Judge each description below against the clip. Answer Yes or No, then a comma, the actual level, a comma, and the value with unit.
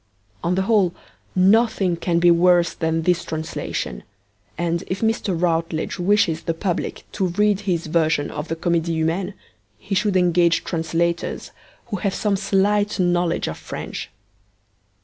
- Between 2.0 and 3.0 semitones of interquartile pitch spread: Yes, average, 2.7 semitones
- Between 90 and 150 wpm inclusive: Yes, average, 145 wpm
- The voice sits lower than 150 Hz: No, medium, 175 Hz